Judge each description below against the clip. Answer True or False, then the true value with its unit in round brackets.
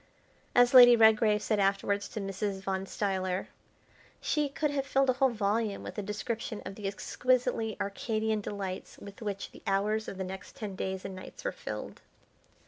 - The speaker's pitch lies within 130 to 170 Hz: False (210 Hz)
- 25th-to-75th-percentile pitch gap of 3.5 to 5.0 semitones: False (3.0 semitones)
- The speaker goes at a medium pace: True (175 wpm)